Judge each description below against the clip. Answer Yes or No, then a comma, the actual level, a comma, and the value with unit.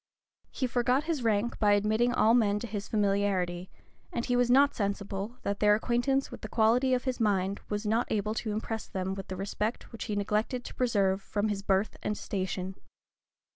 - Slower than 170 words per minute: No, average, 195 wpm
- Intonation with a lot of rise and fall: No, average, 3.2 semitones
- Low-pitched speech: No, high, 210 Hz